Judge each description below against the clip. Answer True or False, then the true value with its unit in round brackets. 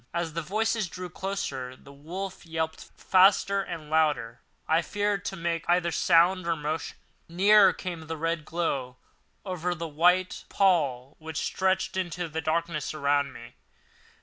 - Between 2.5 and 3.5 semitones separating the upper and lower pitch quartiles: True (3.1 semitones)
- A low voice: False (170 Hz)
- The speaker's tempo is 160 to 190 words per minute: False (150 wpm)